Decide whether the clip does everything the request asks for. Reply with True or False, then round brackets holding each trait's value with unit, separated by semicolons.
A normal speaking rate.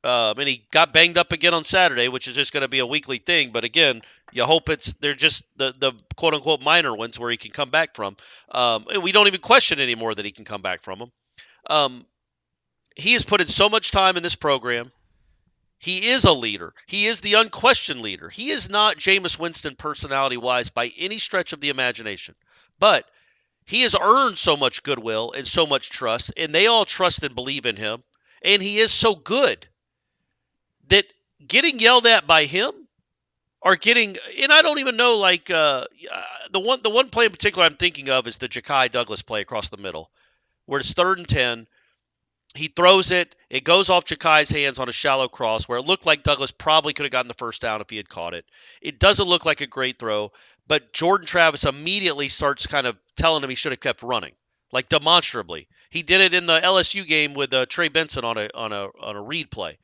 False (220 wpm)